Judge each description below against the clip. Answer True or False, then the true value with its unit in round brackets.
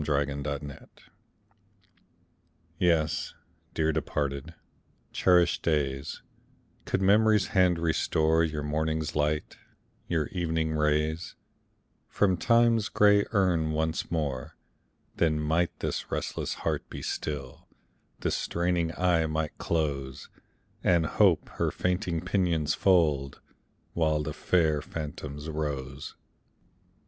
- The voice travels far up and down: False (2.7 semitones)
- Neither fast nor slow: False (100 wpm)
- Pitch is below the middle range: True (80 Hz)